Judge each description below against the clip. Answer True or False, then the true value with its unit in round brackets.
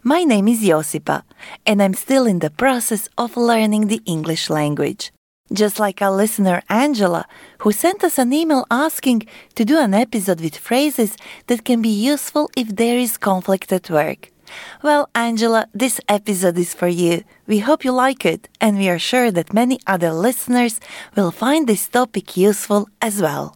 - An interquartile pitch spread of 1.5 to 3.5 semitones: False (4.7 semitones)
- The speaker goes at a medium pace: False (175 wpm)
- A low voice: False (220 Hz)